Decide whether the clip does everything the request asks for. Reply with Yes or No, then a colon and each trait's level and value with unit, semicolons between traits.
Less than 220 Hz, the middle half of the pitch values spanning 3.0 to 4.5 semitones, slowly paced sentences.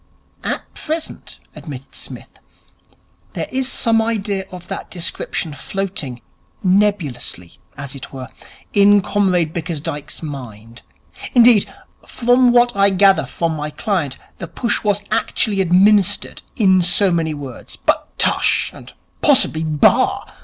No: medium, 185 Hz; wide, 5.5 semitones; slow, 125 wpm